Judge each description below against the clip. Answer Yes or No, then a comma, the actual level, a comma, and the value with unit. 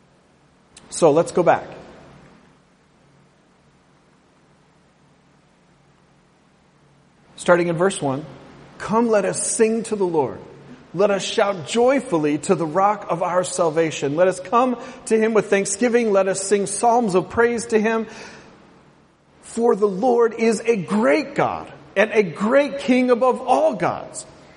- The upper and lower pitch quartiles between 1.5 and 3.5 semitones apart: No, average, 4.7 semitones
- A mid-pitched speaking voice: No, high, 200 Hz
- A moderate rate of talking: No, slow, 130 wpm